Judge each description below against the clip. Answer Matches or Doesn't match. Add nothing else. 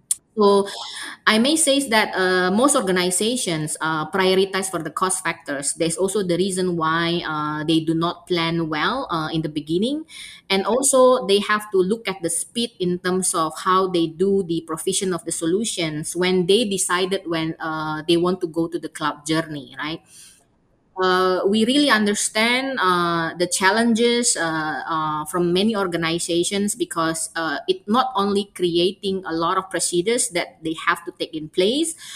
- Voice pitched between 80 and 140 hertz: Doesn't match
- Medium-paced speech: Matches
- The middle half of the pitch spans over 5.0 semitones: Doesn't match